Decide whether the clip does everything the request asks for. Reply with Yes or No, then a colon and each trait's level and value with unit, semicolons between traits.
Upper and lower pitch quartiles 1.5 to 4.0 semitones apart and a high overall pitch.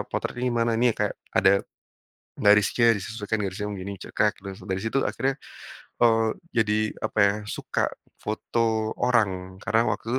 No: narrow, 2.4 semitones; low, 110 Hz